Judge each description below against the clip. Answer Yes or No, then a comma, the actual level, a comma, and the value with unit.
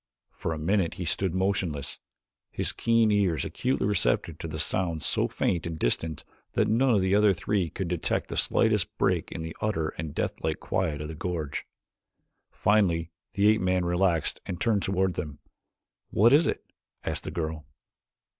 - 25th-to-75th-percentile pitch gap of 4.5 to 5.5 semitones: No, average, 3.9 semitones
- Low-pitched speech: Yes, very low, 90 Hz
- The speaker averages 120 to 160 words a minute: No, average, 170 wpm